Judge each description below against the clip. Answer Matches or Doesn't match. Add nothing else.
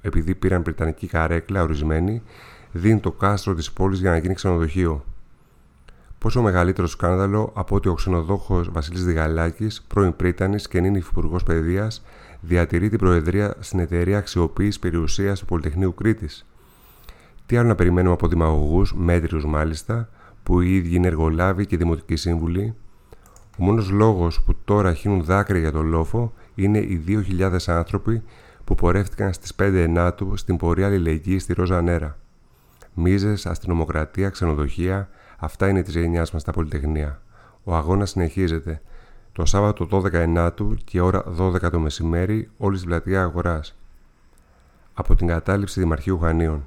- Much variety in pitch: Doesn't match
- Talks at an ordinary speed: Matches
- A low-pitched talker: Matches